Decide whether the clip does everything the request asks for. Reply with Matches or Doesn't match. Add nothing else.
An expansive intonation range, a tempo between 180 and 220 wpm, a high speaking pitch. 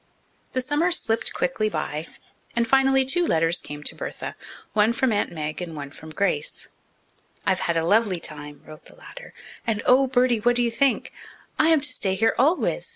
Matches